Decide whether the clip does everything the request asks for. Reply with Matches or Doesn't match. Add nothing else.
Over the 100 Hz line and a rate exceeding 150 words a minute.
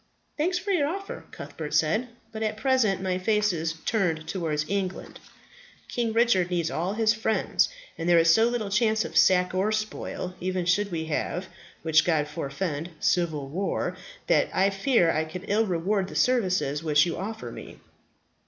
Matches